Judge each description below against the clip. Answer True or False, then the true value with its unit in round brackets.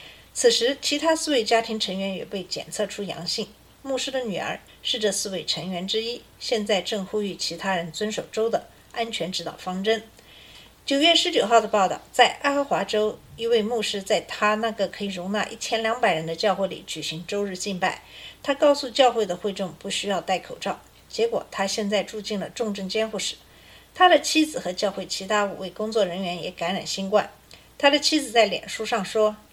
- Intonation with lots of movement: False (3.5 semitones)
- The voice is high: True (210 Hz)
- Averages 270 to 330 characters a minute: True (295 characters per minute)